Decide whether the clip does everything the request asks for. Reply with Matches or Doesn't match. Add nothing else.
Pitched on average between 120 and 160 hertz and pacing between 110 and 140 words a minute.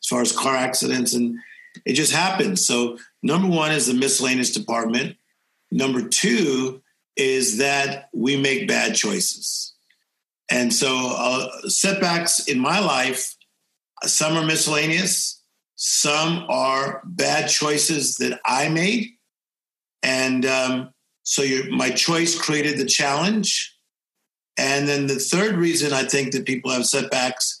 Matches